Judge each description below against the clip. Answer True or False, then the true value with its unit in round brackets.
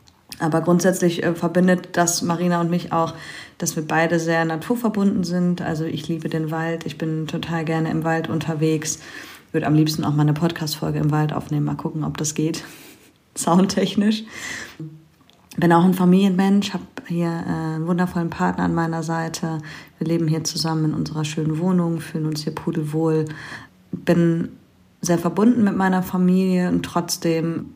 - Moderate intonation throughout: False (1.8 semitones)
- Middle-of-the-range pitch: True (165 Hz)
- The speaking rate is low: False (160 wpm)